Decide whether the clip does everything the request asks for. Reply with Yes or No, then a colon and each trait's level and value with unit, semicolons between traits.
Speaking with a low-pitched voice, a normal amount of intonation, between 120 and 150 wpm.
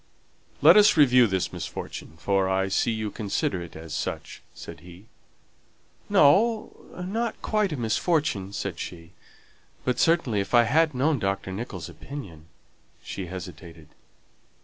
No: low, 110 Hz; wide, 7.9 semitones; average, 140 wpm